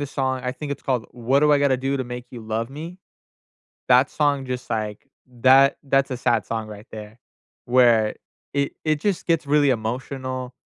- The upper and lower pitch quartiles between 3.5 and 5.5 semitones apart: No, average, 2.9 semitones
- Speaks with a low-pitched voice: Yes, low, 130 Hz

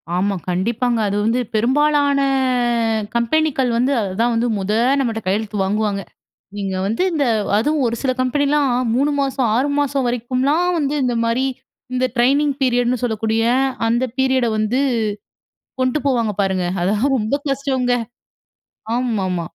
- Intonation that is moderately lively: Yes, average, 4.0 semitones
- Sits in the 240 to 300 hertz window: Yes, high, 245 Hz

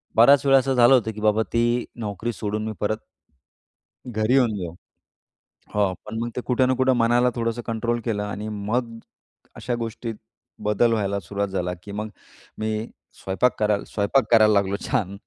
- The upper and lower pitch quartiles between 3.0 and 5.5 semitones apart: No, narrow, 2.5 semitones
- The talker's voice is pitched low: Yes, low, 110 Hz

